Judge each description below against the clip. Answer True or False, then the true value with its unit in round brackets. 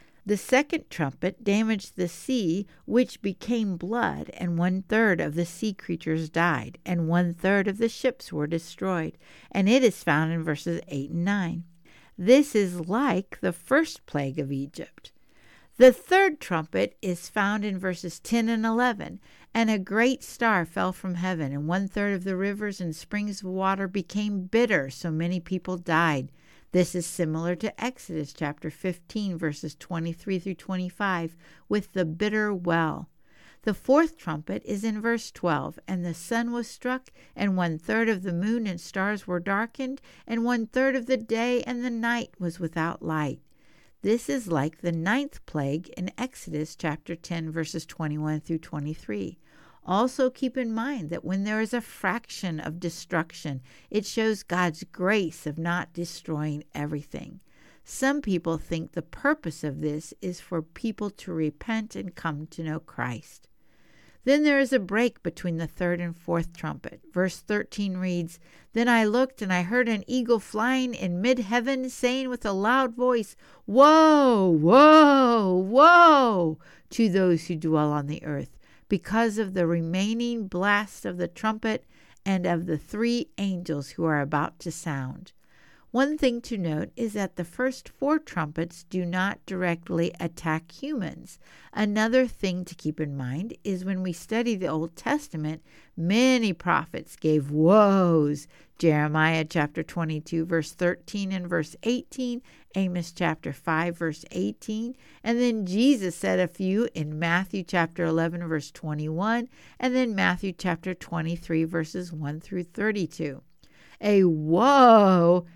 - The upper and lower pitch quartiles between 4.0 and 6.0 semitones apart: True (5.4 semitones)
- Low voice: False (185 Hz)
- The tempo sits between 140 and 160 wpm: True (155 wpm)